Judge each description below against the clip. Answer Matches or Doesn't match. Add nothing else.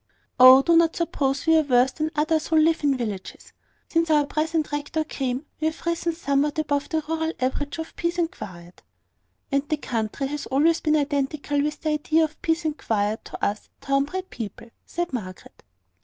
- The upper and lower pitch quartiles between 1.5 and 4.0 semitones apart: Matches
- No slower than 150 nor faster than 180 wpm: Doesn't match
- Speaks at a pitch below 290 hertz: Doesn't match